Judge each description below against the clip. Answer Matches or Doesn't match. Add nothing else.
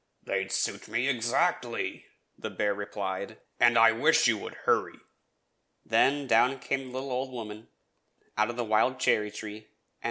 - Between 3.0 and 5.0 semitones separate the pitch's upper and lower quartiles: Matches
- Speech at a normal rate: Matches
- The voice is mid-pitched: Doesn't match